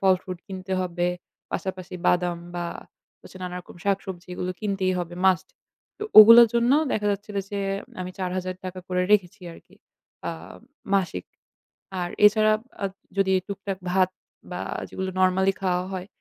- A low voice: No, medium, 185 Hz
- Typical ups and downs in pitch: No, narrow, 1.5 semitones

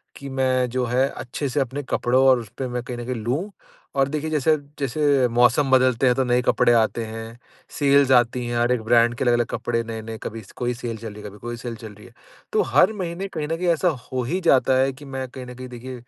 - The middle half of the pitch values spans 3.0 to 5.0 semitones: No, narrow, 2.4 semitones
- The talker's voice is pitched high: No, low, 125 Hz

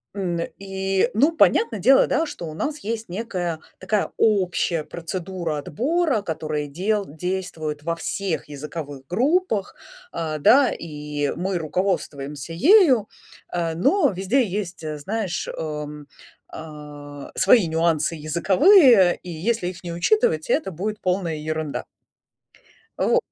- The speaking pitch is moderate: Yes, medium, 180 Hz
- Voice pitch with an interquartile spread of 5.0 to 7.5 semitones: Yes, wide, 5.4 semitones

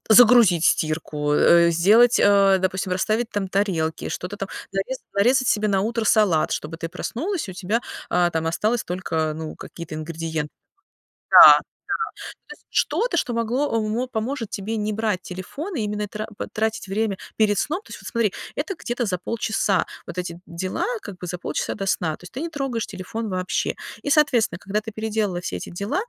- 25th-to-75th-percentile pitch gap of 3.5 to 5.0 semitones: Yes, average, 4.2 semitones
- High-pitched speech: Yes, high, 205 Hz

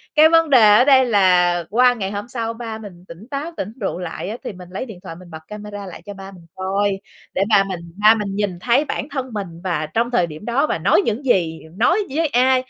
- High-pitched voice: Yes, high, 210 Hz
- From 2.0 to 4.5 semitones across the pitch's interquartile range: No, average, 5.0 semitones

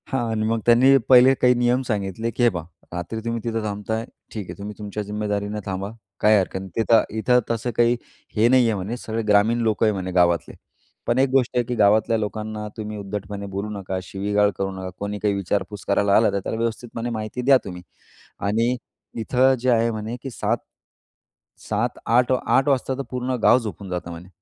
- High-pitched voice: No, low, 110 Hz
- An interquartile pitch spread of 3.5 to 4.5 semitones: No, average, 2.8 semitones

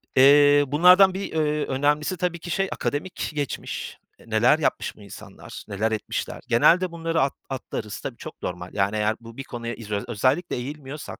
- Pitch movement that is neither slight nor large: No, wide, 5.9 semitones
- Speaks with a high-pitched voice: No, medium, 140 Hz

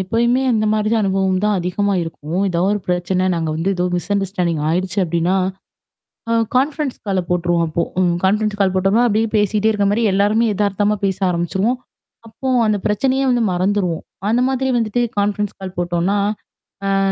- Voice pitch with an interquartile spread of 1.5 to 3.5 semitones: Yes, average, 3.1 semitones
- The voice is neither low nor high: No, high, 195 Hz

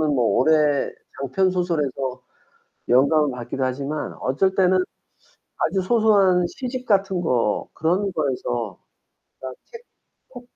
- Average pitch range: No, wide, 6.5 semitones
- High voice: No, medium, 155 Hz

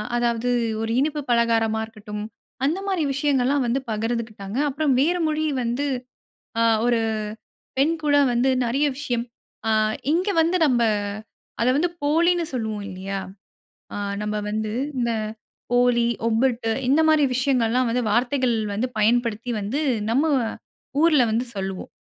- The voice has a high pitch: Yes, high, 245 Hz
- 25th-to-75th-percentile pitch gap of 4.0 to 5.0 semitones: Yes, average, 4.3 semitones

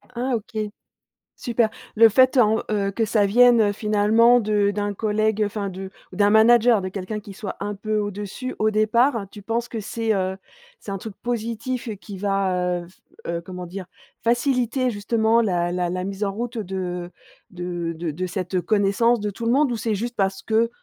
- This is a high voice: Yes, high, 210 Hz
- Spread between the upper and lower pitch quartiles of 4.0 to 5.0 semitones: No, average, 3.1 semitones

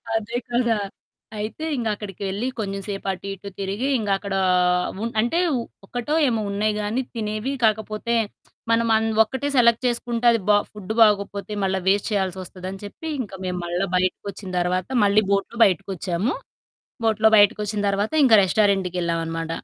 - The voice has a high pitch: Yes, high, 205 Hz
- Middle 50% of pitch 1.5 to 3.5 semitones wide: Yes, average, 2.9 semitones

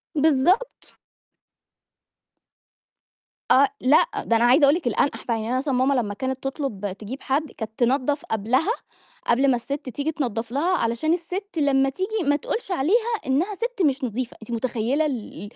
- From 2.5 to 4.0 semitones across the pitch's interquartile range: No, average, 4.6 semitones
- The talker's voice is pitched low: No, very high, 270 Hz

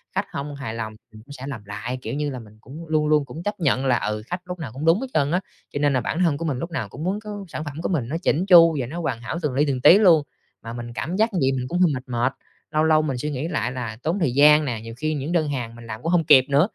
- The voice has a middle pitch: Yes, medium, 145 Hz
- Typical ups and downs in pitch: Yes, average, 4.8 semitones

